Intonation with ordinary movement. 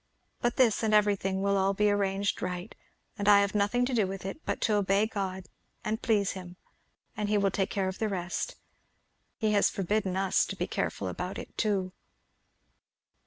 No: narrow, 1.7 semitones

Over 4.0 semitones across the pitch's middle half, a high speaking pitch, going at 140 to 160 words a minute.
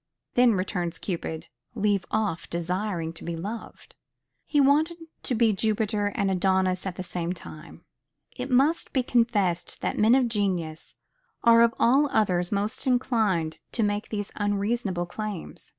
Yes: average, 4.4 semitones; high, 205 Hz; average, 150 wpm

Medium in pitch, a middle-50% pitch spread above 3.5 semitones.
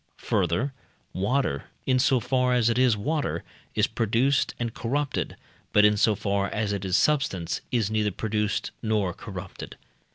No: low, 110 Hz; average, 3.9 semitones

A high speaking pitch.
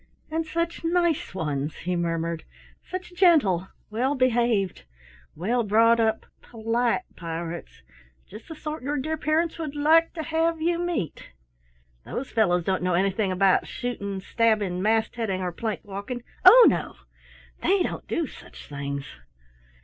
Yes: high, 230 Hz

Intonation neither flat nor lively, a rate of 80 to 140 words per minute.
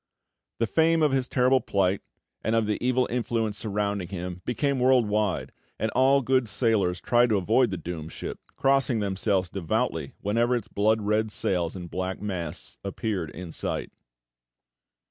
No: average, 4.6 semitones; average, 160 wpm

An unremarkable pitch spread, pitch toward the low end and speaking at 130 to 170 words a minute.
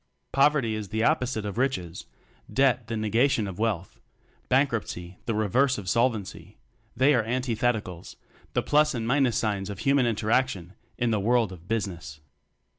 Yes: average, 4.1 semitones; low, 115 Hz; average, 155 wpm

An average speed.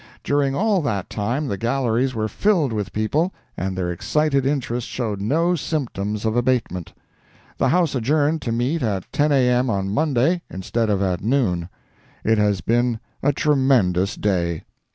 Yes: average, 160 wpm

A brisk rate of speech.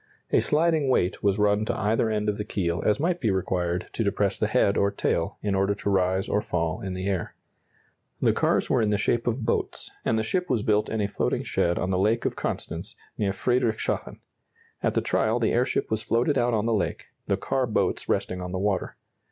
Yes: fast, 225 wpm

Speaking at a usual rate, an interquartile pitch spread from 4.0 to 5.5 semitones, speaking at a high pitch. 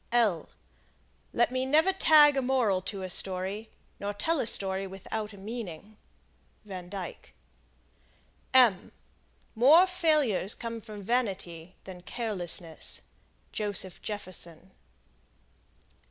No: slow, 105 wpm; average, 4.6 semitones; high, 205 Hz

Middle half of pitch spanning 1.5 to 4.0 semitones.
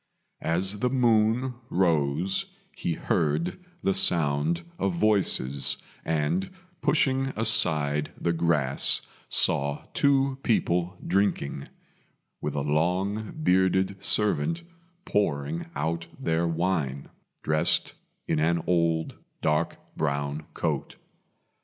No: average, 4.8 semitones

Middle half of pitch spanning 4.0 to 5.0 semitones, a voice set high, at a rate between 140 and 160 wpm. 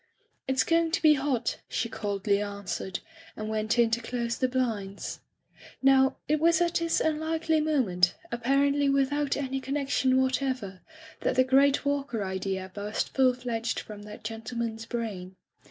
Yes: average, 4.7 semitones; very high, 250 Hz; average, 155 wpm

